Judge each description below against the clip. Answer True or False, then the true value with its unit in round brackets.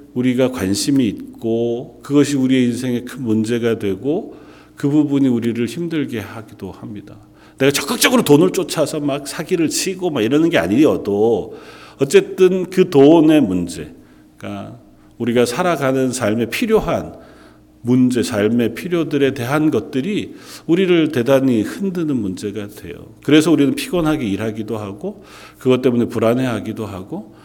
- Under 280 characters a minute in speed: False (320 characters per minute)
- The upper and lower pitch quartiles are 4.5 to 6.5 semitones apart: True (5.6 semitones)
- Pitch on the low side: True (130 Hz)